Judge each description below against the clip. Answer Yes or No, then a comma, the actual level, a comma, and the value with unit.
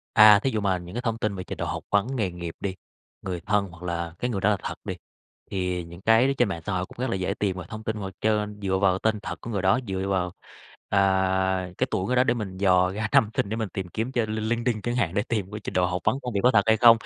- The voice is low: Yes, low, 100 Hz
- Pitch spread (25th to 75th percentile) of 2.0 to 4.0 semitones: Yes, average, 3.0 semitones